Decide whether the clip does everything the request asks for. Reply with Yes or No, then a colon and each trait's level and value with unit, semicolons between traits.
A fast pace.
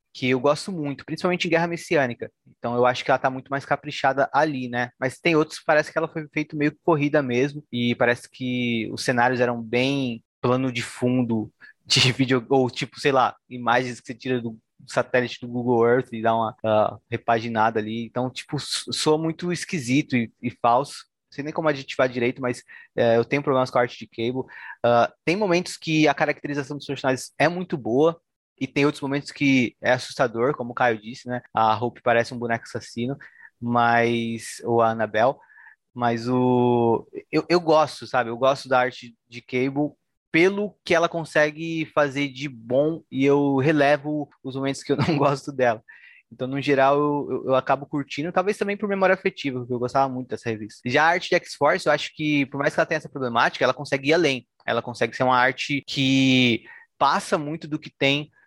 Yes: fast, 200 wpm